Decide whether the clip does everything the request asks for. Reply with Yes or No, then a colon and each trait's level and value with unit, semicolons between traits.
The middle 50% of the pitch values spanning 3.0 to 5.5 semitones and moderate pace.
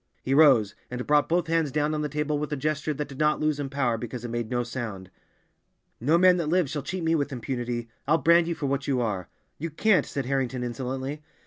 No: average, 3.7 semitones; fast, 235 wpm